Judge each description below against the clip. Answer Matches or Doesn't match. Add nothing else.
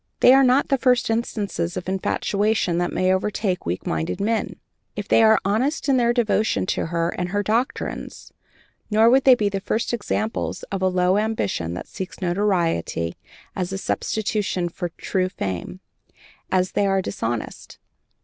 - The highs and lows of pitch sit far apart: Doesn't match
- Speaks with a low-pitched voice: Doesn't match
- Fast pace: Doesn't match